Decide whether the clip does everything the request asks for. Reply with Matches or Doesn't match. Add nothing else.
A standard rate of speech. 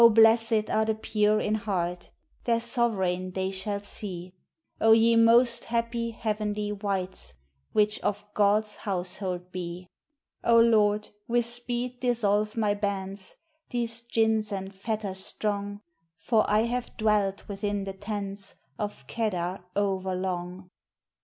Doesn't match